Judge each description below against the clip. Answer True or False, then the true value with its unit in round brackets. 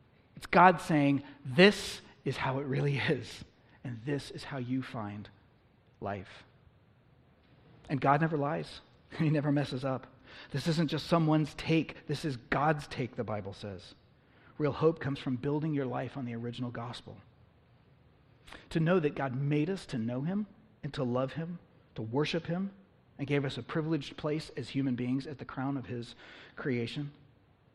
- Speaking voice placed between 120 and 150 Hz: True (135 Hz)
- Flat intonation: False (3.7 semitones)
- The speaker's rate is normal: True (170 wpm)